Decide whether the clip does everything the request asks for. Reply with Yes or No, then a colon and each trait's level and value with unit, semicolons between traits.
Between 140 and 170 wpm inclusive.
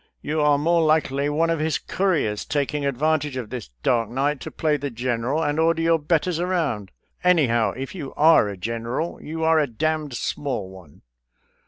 No: average, 185 wpm